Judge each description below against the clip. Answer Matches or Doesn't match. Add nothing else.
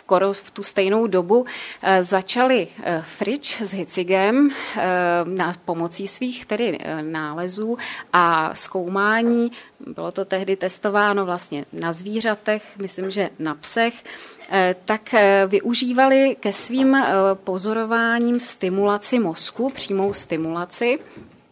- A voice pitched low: Doesn't match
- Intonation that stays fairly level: Doesn't match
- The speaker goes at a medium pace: Doesn't match